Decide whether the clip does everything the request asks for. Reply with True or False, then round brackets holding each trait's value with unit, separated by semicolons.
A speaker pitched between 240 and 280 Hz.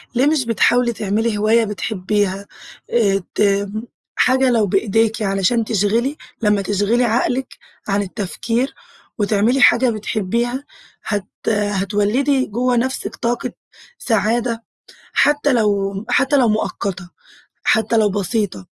False (220 Hz)